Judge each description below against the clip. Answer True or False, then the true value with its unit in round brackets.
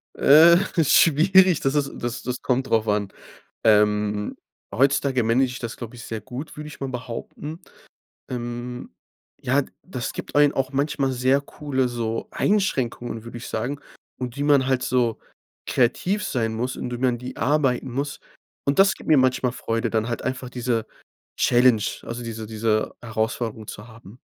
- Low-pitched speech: True (125 Hz)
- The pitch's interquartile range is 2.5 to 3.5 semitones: True (3.2 semitones)